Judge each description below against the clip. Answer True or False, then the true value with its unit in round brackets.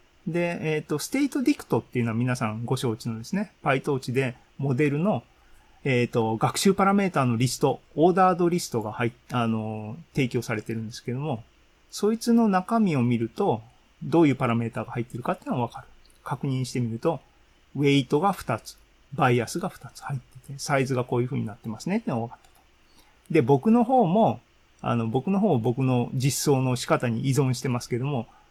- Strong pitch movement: True (5.7 semitones)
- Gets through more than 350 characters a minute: True (395 characters per minute)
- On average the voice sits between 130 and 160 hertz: True (135 Hz)